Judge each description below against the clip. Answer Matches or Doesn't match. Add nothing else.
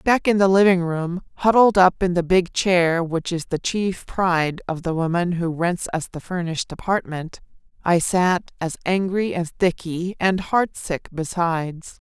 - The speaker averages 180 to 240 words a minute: Doesn't match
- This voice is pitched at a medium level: Matches